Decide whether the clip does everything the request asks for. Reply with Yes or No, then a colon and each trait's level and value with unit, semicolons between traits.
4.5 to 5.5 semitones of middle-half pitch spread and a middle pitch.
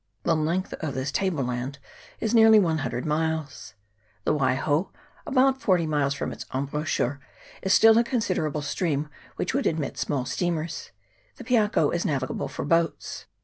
Yes: average, 5.0 semitones; medium, 155 Hz